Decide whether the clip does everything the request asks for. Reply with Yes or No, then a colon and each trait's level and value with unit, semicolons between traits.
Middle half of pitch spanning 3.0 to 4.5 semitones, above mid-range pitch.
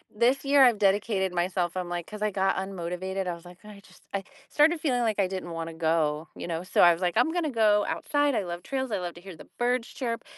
No: average, 5.2 semitones; high, 195 Hz